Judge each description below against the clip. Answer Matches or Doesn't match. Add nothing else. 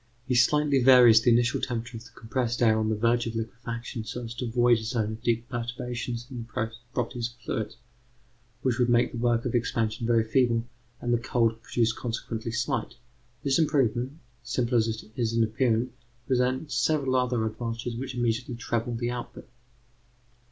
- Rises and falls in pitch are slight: Matches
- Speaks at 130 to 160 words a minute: Doesn't match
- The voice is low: Matches